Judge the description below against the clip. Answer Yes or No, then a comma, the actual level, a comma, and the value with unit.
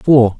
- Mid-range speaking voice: No, low, 120 Hz